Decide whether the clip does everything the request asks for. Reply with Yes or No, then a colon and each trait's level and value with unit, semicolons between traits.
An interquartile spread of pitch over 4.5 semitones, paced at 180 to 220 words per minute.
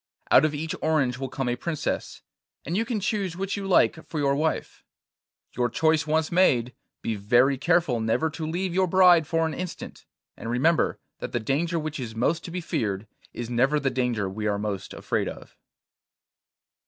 Yes: wide, 5.6 semitones; average, 190 wpm